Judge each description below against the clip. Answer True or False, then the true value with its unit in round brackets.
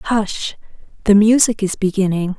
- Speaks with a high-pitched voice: True (205 Hz)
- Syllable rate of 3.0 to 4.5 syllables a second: True (4.3 syllables/s)